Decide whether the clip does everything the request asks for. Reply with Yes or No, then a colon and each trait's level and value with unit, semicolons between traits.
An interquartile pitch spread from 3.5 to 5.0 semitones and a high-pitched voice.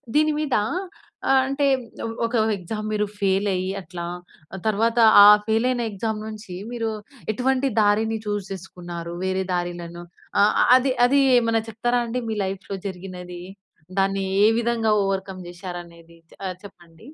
Yes: average, 4.0 semitones; high, 200 Hz